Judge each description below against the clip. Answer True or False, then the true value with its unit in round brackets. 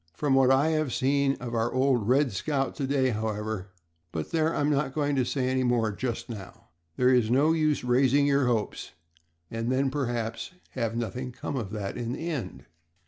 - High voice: False (130 Hz)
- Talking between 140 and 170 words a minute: False (195 wpm)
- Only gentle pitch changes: False (3.3 semitones)